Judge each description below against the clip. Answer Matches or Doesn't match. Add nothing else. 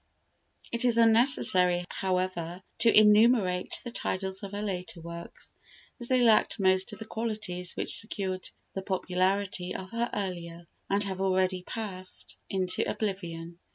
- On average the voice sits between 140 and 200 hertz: Matches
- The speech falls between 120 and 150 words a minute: Matches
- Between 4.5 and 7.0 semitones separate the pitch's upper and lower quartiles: Doesn't match